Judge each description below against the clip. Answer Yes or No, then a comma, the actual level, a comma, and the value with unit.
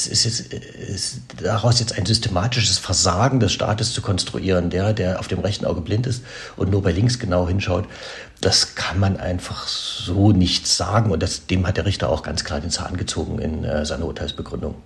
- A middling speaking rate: No, fast, 195 wpm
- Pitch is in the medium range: No, very low, 95 Hz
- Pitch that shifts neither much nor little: Yes, average, 3.6 semitones